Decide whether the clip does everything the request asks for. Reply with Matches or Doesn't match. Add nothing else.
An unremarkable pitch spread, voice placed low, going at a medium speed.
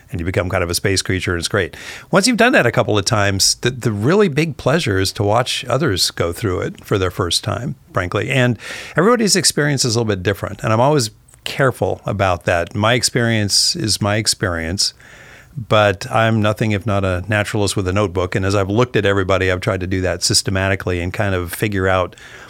Doesn't match